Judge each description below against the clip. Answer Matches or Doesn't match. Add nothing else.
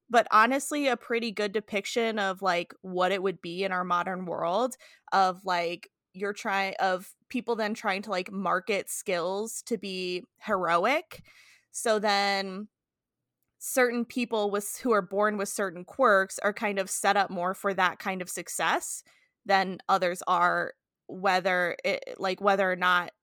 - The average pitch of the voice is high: Matches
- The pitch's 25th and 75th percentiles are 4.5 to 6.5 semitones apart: Doesn't match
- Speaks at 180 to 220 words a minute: Doesn't match